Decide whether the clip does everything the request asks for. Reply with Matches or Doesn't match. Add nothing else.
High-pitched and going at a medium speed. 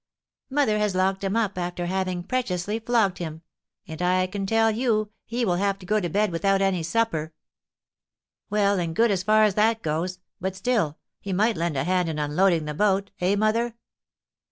Matches